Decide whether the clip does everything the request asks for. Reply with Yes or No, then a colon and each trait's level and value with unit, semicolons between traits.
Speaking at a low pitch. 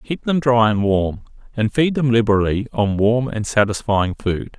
Yes: low, 115 Hz